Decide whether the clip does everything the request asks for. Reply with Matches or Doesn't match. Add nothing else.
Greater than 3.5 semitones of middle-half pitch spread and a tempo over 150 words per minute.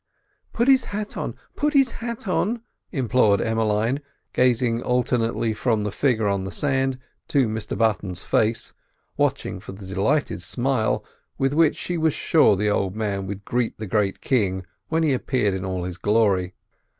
Matches